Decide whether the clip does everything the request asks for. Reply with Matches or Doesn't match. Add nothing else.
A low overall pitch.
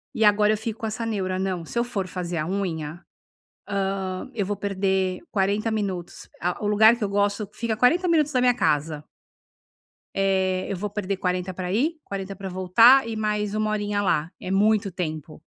Doesn't match